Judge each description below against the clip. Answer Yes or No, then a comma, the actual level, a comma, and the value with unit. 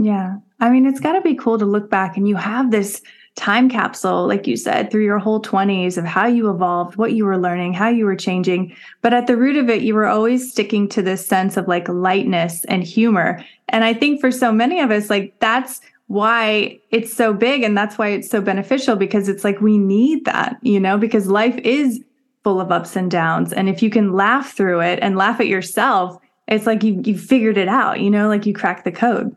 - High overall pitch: Yes, high, 215 Hz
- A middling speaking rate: No, fast, 235 wpm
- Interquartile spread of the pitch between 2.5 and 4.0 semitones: Yes, average, 3.3 semitones